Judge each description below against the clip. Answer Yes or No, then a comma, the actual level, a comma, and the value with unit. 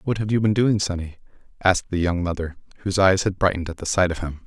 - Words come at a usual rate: No, fast, 255 wpm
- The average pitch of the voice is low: Yes, very low, 95 Hz